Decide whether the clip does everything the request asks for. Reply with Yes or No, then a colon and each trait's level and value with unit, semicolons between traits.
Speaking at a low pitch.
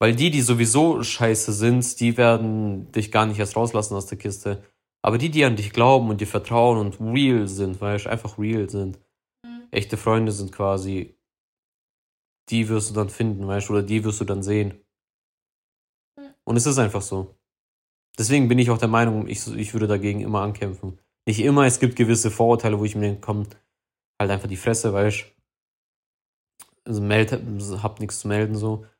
Yes: low, 110 Hz